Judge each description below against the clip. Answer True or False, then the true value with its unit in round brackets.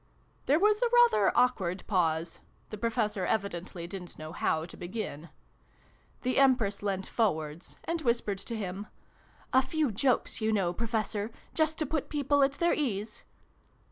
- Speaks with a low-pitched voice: False (215 Hz)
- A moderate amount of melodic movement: False (6.3 semitones)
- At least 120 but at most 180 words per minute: True (155 wpm)